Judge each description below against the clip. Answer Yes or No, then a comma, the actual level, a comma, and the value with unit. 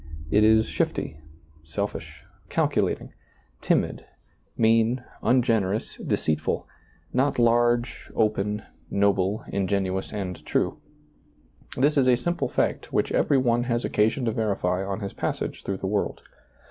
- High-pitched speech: No, low, 110 Hz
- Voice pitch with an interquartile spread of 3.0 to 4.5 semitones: Yes, average, 3.5 semitones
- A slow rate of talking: Yes, slow, 125 wpm